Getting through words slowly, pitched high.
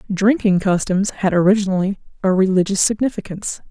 Yes: slow, 115 wpm; high, 195 Hz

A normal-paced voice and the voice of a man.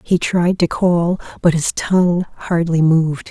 No: average, 165 wpm; female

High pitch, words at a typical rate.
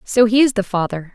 No: high, 215 Hz; fast, 260 wpm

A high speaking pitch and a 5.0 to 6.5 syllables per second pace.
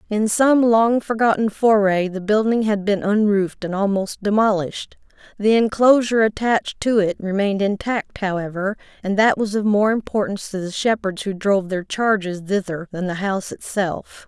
Yes: high, 205 Hz; 5.1 syllables/s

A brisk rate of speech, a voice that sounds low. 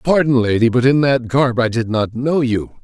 Yes: fast, 230 wpm; low, 125 Hz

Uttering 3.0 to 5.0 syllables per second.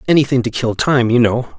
No: 5.8 syllables/s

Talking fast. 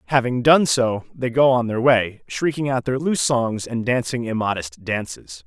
No: average, 185 wpm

